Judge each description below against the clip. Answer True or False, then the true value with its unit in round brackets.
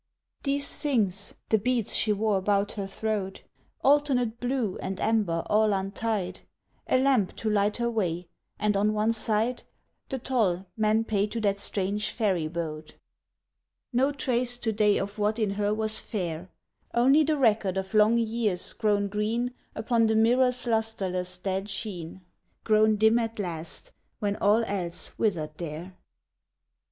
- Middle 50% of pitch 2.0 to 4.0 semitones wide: True (2.9 semitones)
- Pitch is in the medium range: False (215 Hz)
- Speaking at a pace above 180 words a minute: False (150 wpm)